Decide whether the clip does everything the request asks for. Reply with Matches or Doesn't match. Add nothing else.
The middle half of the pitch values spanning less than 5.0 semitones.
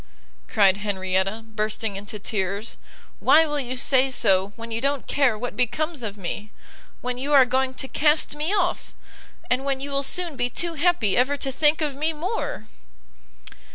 Doesn't match